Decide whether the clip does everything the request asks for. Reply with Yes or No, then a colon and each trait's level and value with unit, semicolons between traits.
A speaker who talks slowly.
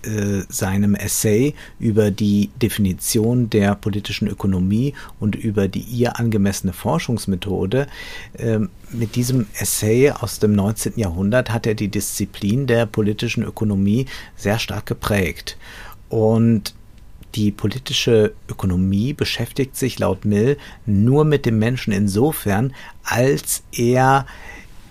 Yes: slow, 110 wpm